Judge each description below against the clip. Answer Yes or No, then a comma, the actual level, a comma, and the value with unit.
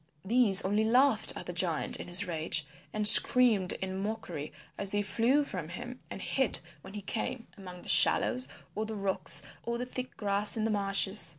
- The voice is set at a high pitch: Yes, high, 205 Hz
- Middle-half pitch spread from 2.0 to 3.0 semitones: No, average, 3.4 semitones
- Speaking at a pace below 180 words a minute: No, average, 190 wpm